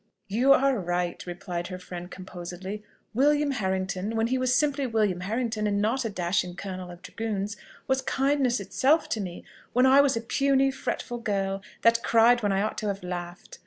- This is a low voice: No, high, 210 Hz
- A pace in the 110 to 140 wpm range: No, average, 185 wpm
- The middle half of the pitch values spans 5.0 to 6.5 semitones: Yes, wide, 5.4 semitones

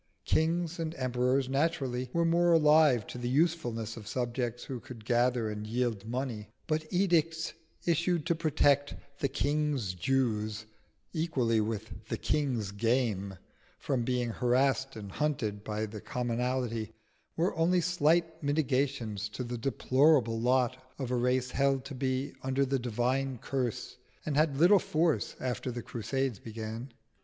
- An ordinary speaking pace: Yes, average, 145 wpm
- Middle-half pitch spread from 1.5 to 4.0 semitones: No, average, 4.4 semitones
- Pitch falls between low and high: No, low, 130 Hz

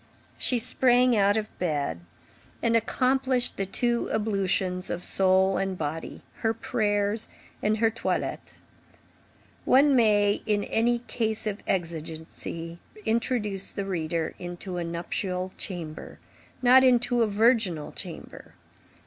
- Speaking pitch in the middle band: No, high, 205 Hz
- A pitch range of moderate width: Yes, average, 4.3 semitones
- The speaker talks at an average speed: No, slow, 120 wpm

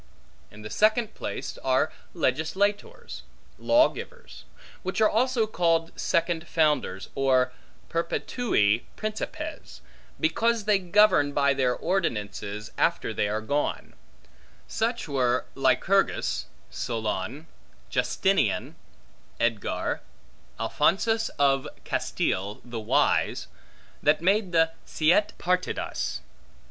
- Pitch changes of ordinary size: No, wide, 8.7 semitones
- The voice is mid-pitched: Yes, medium, 160 Hz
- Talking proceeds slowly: Yes, slow, 95 wpm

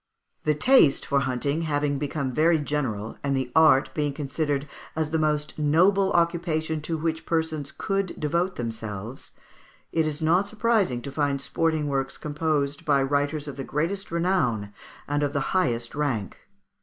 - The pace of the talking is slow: No, average, 160 wpm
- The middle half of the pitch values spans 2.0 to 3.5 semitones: Yes, average, 2.8 semitones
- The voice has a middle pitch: Yes, medium, 150 Hz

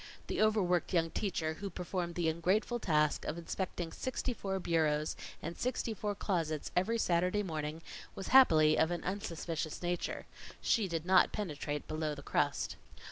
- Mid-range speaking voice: Yes, medium, 175 Hz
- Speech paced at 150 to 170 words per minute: Yes, average, 155 wpm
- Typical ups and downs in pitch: Yes, average, 3.7 semitones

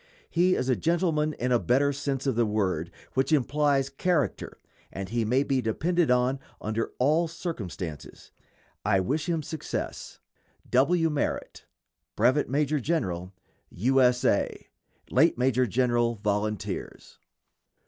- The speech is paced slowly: Yes, slow, 130 wpm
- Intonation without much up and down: No, average, 5.0 semitones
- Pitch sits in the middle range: No, low, 130 Hz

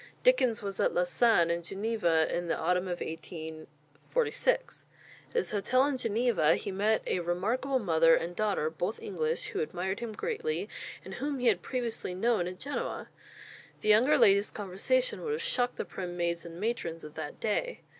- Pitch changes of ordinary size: No, wide, 6.4 semitones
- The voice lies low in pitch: No, high, 200 Hz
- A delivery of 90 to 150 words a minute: No, average, 175 wpm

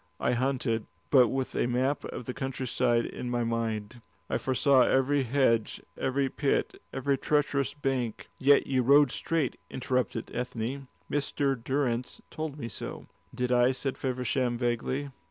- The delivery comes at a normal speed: Yes, average, 150 wpm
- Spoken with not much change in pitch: Yes, narrow, 2.3 semitones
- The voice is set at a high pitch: No, low, 130 Hz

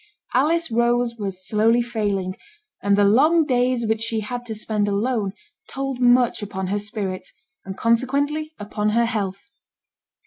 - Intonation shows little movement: No, average, 3.2 semitones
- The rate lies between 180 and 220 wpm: No, average, 145 wpm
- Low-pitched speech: No, high, 225 Hz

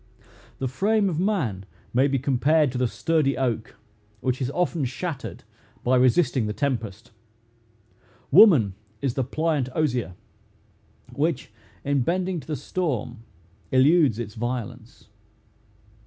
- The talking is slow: Yes, slow, 125 wpm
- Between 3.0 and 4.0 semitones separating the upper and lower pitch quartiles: No, average, 4.7 semitones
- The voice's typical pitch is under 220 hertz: Yes, low, 135 Hz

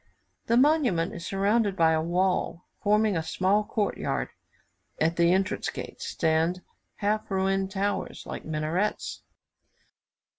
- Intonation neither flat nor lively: Yes, average, 3.7 semitones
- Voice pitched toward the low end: No, high, 190 Hz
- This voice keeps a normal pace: No, slow, 125 wpm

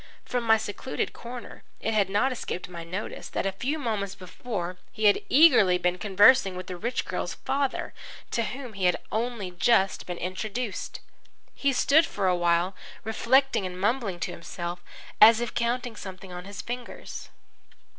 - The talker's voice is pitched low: No, high, 205 Hz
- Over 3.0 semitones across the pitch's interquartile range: Yes, average, 4.7 semitones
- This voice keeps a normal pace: Yes, average, 170 wpm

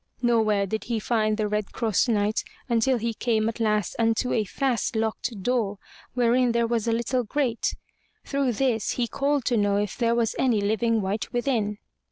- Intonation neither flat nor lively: No, narrow, 2.2 semitones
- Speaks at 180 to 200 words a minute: Yes, average, 185 wpm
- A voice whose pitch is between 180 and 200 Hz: No, high, 230 Hz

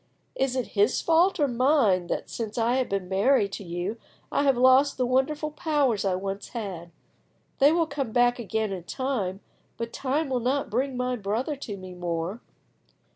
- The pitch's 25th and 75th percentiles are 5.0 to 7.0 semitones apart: Yes, wide, 5.5 semitones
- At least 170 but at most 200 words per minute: Yes, average, 185 wpm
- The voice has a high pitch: Yes, high, 245 Hz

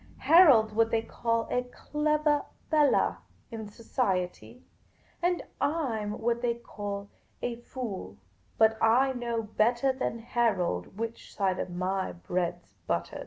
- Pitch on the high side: Yes, high, 230 Hz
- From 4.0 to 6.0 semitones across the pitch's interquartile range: No, average, 3.6 semitones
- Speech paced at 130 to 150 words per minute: Yes, average, 140 wpm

